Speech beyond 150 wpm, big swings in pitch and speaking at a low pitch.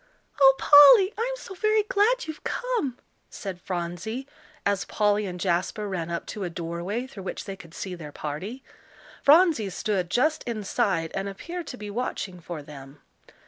No: average, 165 wpm; wide, 8.2 semitones; high, 205 Hz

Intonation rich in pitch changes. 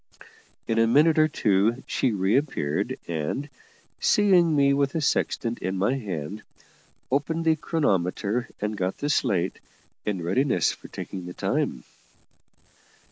Yes: wide, 7.3 semitones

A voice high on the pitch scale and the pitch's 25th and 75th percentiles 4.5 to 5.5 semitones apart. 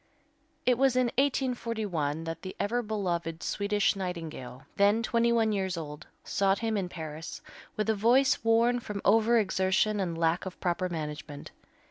Yes: high, 200 Hz; average, 5.2 semitones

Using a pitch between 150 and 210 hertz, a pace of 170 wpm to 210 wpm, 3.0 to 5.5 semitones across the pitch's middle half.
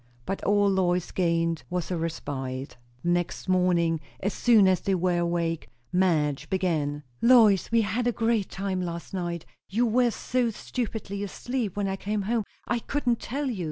Yes: high, 190 Hz; average, 175 wpm; average, 4.4 semitones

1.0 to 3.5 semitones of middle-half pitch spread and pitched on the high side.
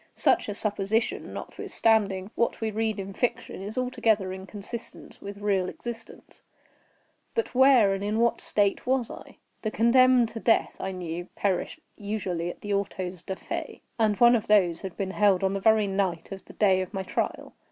Yes: average, 2.8 semitones; high, 205 Hz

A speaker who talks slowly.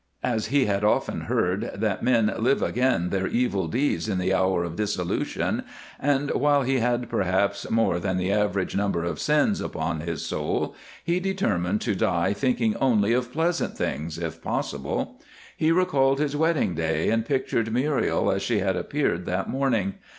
No: average, 170 wpm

